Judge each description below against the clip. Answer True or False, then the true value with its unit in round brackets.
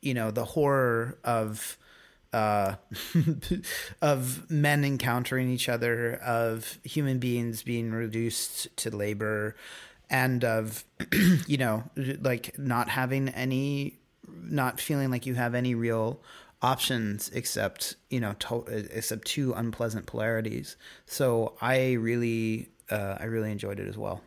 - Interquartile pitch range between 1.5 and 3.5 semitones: True (2.9 semitones)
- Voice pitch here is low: True (120 Hz)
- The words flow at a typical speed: False (130 wpm)